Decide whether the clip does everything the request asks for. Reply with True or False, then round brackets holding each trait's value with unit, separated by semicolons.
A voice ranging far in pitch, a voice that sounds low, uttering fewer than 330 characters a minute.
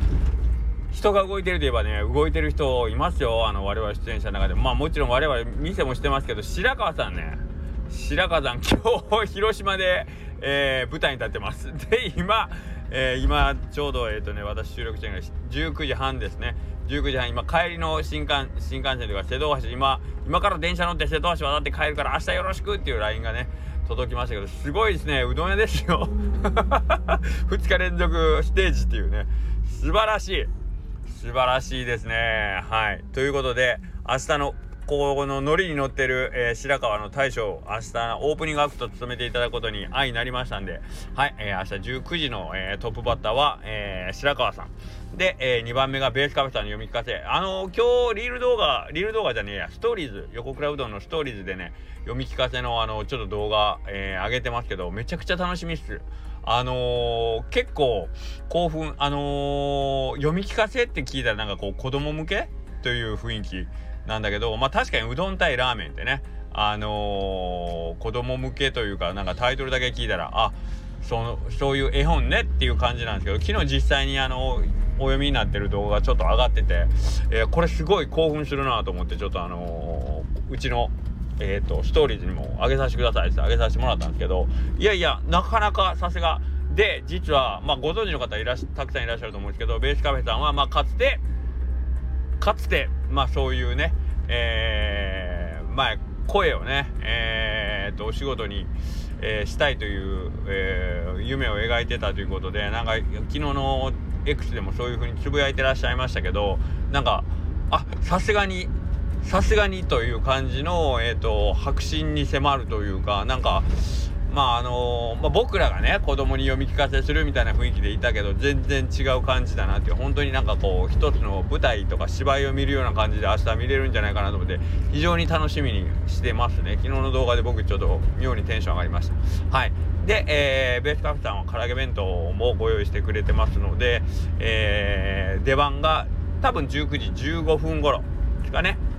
False (8.1 semitones; 85 Hz; 390 characters per minute)